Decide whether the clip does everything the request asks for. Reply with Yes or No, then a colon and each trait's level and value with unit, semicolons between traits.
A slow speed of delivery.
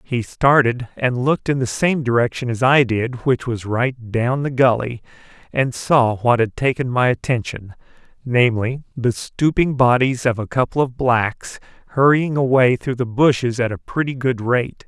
No: average, 175 wpm